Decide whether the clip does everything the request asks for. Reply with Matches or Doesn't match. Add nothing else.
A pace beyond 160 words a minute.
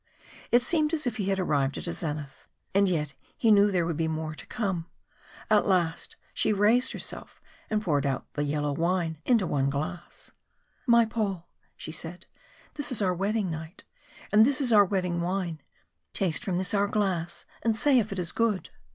Matches